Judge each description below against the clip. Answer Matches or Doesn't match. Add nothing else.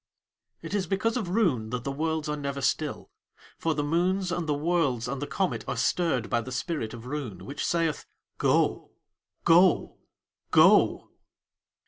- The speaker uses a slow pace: Doesn't match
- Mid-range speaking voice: Matches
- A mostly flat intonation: Doesn't match